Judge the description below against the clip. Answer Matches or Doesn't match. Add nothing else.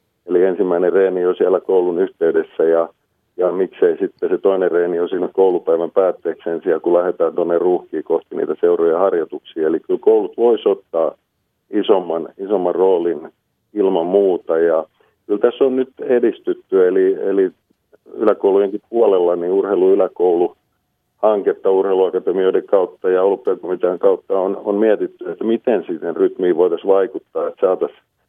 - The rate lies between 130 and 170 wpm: Matches